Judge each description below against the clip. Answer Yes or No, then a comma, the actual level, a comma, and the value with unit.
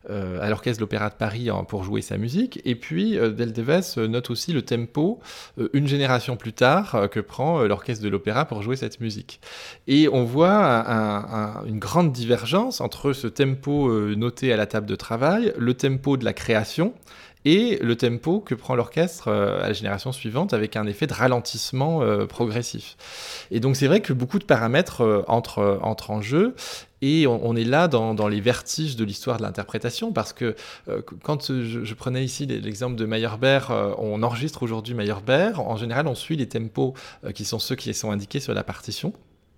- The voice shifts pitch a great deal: No, average, 4.1 semitones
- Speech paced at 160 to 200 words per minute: Yes, average, 185 wpm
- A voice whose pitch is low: Yes, low, 120 Hz